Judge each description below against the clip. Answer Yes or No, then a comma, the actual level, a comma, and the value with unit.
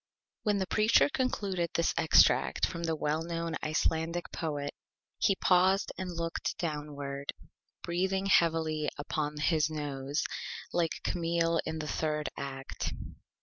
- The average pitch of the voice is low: No, medium, 165 Hz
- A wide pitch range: No, narrow, 2.5 semitones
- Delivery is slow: Yes, slow, 125 wpm